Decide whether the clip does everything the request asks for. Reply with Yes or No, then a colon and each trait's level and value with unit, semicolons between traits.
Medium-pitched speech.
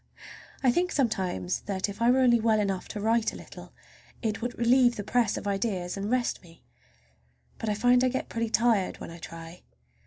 No: high, 220 Hz